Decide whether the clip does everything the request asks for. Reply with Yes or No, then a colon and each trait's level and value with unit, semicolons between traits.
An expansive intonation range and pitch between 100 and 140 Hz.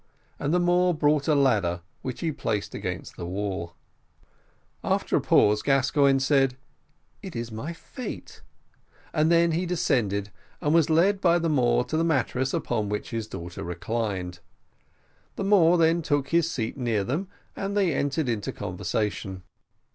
Yes: wide, 7.4 semitones; low, 135 Hz